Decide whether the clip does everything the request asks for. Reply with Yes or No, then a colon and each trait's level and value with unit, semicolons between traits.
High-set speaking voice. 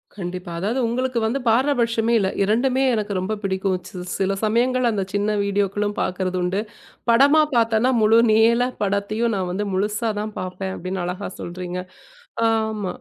Yes: high, 210 Hz